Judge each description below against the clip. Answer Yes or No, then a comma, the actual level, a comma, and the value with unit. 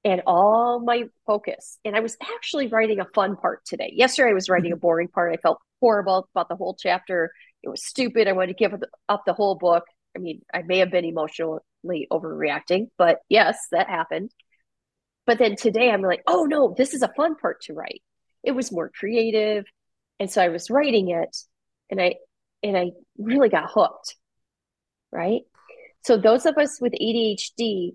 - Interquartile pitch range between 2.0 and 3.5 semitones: No, average, 5.0 semitones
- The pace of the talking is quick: No, average, 190 wpm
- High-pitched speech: Yes, high, 210 Hz